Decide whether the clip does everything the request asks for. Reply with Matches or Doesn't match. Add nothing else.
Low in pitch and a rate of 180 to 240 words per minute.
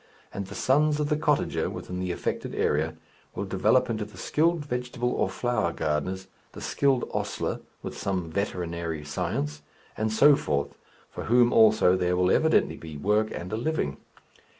Doesn't match